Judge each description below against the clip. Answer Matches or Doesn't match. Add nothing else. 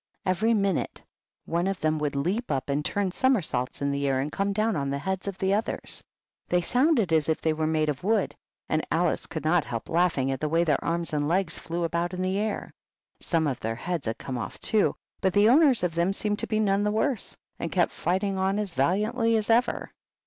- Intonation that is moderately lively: Matches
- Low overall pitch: Doesn't match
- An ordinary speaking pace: Doesn't match